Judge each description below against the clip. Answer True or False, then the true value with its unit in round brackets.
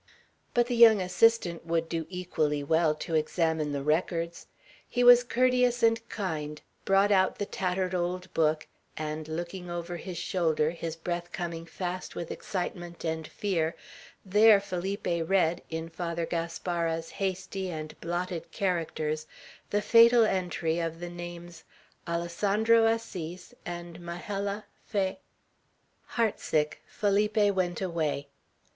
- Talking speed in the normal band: False (130 wpm)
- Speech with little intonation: False (3.2 semitones)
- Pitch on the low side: False (175 Hz)